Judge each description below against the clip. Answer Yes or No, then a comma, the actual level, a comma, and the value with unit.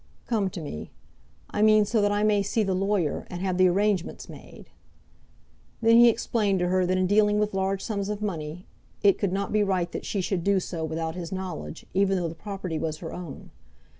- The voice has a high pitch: Yes, high, 195 Hz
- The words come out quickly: Yes, fast, 215 wpm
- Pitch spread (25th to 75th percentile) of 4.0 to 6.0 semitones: No, narrow, 2.6 semitones